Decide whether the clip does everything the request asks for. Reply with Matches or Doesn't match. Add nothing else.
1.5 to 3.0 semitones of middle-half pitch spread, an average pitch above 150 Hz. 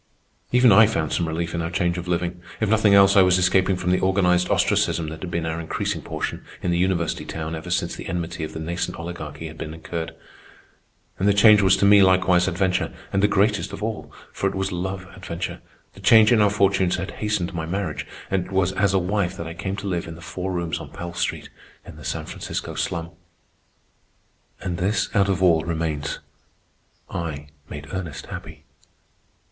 Doesn't match